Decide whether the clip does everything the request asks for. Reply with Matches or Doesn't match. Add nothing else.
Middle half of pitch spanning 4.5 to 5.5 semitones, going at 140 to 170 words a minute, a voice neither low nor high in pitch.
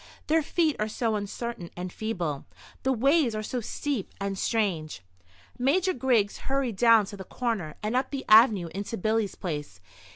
Doesn't match